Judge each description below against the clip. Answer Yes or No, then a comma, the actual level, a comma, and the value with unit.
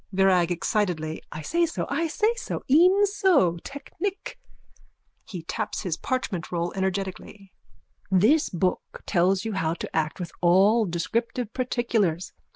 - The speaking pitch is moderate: No, high, 195 Hz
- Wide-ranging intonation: Yes, wide, 6.7 semitones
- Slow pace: Yes, slow, 130 wpm